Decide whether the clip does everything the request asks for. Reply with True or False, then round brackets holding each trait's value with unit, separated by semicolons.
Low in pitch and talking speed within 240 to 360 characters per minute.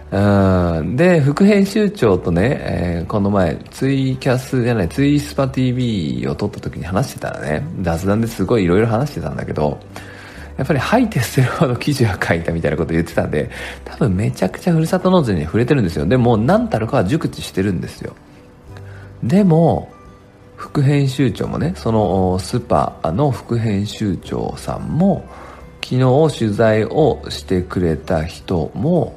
True (110 Hz; 325 characters per minute)